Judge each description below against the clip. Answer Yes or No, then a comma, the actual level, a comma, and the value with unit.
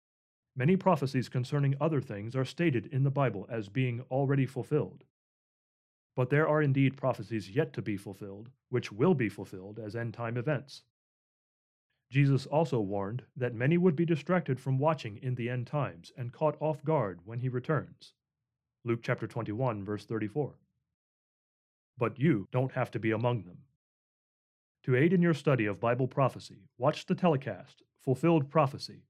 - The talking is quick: No, average, 160 wpm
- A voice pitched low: Yes, low, 130 Hz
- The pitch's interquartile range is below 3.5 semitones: No, average, 4.2 semitones